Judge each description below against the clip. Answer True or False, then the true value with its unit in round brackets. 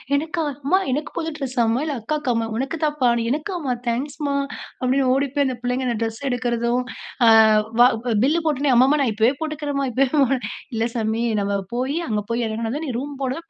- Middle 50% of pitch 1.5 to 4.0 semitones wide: True (3.6 semitones)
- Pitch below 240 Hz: False (260 Hz)